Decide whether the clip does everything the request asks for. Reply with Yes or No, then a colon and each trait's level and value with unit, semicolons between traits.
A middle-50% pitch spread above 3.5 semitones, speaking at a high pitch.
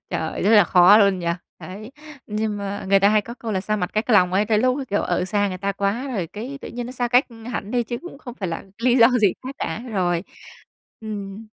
No: average, 3.2 semitones; high, 210 Hz